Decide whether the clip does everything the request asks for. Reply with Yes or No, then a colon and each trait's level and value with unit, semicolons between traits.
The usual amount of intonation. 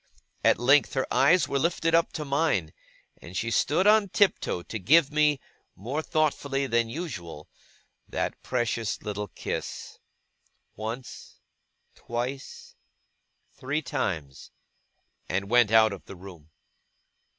No: wide, 6.6 semitones